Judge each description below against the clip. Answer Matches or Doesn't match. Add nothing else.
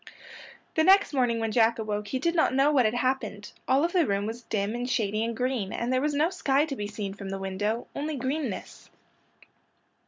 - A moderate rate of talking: Doesn't match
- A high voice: Matches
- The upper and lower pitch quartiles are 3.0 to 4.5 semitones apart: Doesn't match